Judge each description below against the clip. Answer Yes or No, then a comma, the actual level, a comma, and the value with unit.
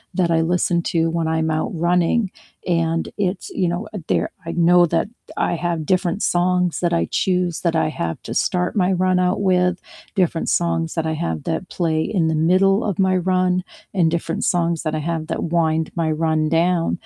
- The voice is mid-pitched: Yes, medium, 170 Hz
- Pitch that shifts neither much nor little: No, narrow, 2.0 semitones